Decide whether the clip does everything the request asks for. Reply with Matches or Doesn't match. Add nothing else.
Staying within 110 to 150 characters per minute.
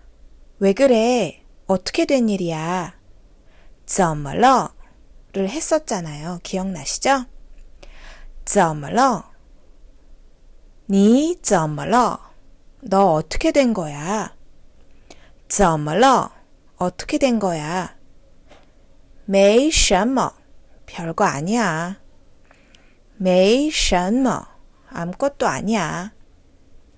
Matches